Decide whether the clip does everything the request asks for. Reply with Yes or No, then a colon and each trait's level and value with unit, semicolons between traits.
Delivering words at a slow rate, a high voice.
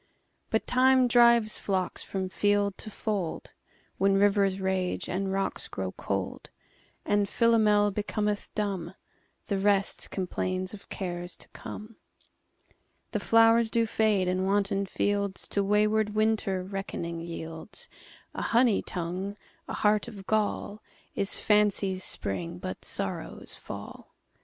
Yes: slow, 110 wpm; high, 200 Hz